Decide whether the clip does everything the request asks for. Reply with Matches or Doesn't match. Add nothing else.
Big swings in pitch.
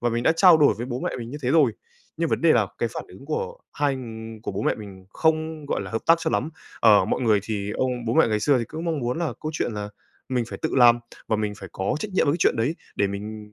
Matches